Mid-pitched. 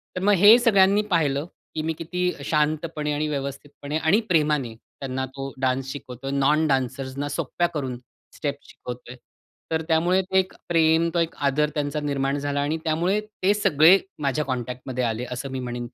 Yes: medium, 145 Hz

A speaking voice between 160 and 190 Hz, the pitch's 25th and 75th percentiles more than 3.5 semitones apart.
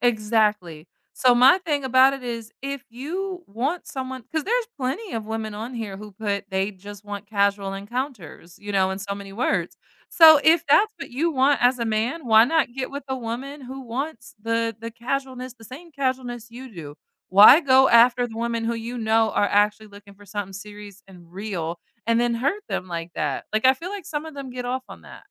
No: high, 235 Hz; average, 4.3 semitones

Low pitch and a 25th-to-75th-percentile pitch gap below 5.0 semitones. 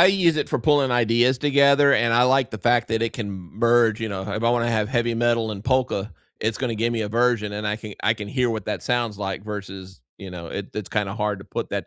Yes: low, 115 Hz; average, 2.8 semitones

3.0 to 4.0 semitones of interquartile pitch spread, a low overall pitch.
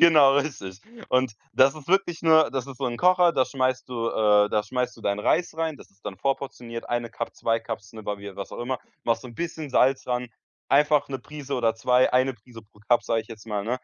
Yes: average, 3.6 semitones; low, 125 Hz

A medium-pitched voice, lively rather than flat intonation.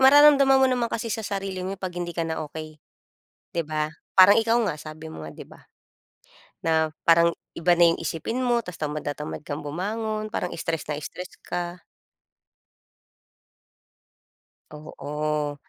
Yes: medium, 175 Hz; wide, 5.7 semitones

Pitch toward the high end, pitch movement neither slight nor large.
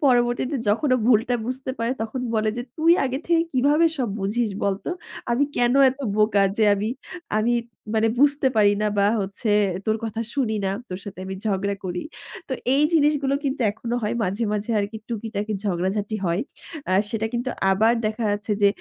Yes: high, 225 Hz; average, 3.9 semitones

